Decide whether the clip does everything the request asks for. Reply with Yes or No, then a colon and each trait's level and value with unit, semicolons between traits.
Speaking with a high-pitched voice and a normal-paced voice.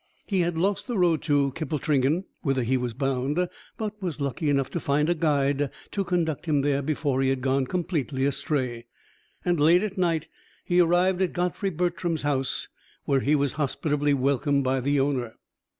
No: medium, 145 Hz; average, 180 wpm